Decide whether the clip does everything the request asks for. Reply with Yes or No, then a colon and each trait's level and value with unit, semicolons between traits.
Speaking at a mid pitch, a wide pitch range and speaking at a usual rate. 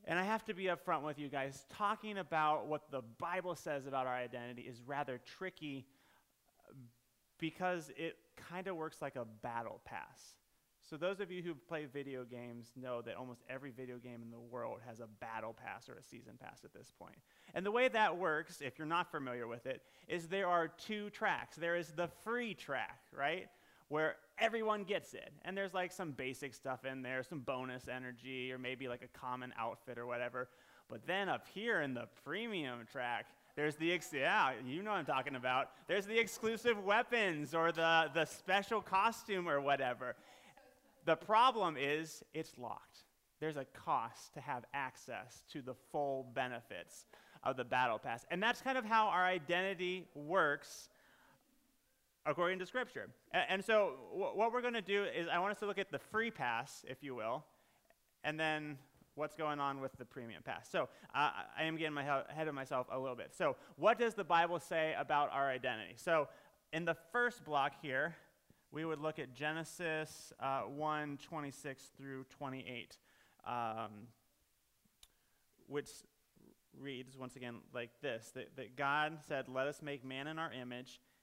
Yes: medium, 150 Hz; wide, 5.7 semitones; average, 185 wpm